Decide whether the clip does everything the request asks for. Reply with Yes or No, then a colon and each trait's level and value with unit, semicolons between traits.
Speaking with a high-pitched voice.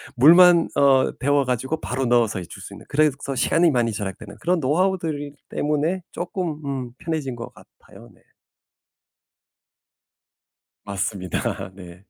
No: medium, 140 Hz